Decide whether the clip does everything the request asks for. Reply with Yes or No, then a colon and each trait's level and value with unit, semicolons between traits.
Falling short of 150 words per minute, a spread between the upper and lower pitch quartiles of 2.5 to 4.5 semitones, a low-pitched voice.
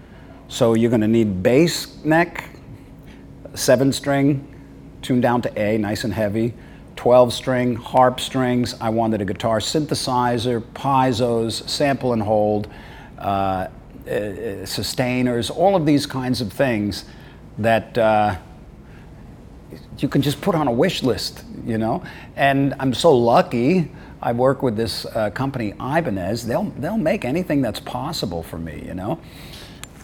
Yes: average, 140 wpm; average, 3.7 semitones; low, 120 Hz